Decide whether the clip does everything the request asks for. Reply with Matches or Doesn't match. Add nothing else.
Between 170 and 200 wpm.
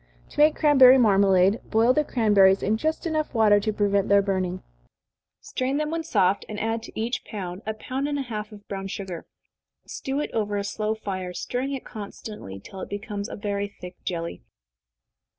Matches